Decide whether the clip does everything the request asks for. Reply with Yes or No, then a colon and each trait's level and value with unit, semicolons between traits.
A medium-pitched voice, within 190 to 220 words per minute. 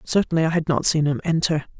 No: medium, 160 Hz; fast, 235 wpm